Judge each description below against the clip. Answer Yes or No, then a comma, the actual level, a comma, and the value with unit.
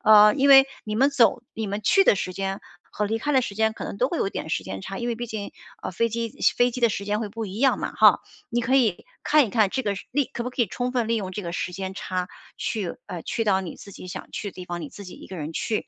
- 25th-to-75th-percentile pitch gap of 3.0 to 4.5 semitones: Yes, average, 3.9 semitones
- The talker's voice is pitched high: Yes, high, 215 Hz